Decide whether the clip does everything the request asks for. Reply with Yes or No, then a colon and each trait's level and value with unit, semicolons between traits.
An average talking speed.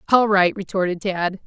Yes: average, 165 wpm